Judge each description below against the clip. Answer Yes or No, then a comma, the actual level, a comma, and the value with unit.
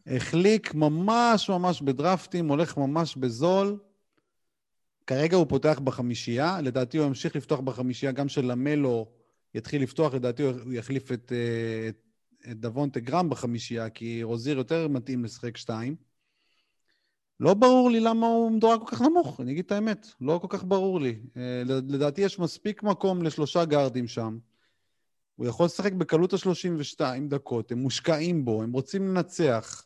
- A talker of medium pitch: Yes, medium, 145 Hz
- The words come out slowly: No, average, 145 wpm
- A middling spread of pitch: No, wide, 6.4 semitones